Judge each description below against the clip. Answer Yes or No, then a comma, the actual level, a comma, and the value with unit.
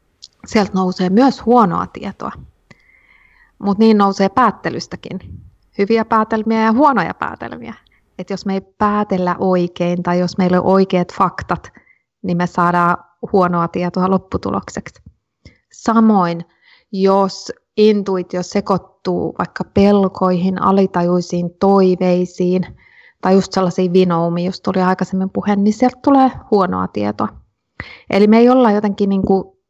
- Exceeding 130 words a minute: No, average, 120 wpm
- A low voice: No, high, 190 Hz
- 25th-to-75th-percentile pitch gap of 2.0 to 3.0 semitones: Yes, narrow, 2.5 semitones